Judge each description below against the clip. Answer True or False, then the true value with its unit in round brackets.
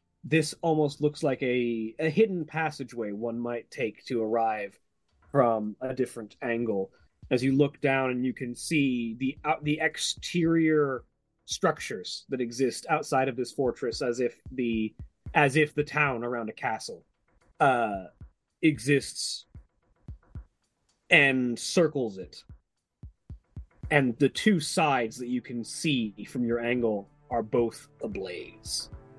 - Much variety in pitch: False (4.0 semitones)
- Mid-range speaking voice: False (130 Hz)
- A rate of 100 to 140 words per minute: True (135 wpm)